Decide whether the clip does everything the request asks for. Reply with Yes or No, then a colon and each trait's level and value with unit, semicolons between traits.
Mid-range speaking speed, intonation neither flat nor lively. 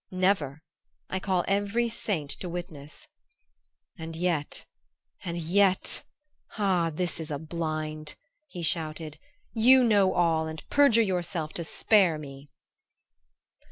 No: slow, 120 wpm; average, 3.8 semitones